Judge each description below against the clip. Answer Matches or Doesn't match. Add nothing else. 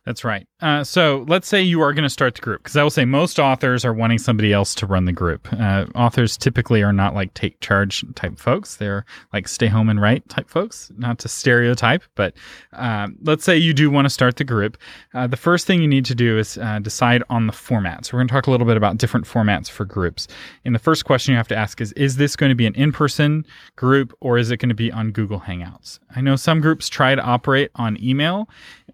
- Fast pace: Matches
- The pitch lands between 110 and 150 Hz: Matches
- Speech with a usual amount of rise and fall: Matches